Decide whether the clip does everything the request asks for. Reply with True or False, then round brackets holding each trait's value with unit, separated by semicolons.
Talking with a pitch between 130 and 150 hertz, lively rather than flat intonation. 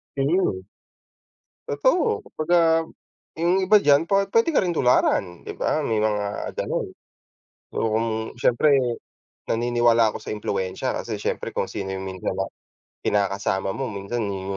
False (120 Hz; 8.4 semitones)